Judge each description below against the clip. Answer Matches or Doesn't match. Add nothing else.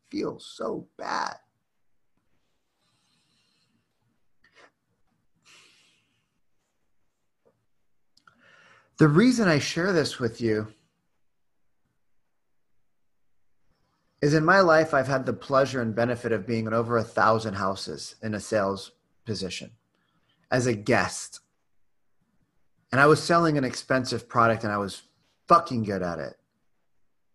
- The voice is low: Matches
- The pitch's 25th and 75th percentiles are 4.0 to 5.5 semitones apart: Matches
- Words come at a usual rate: Doesn't match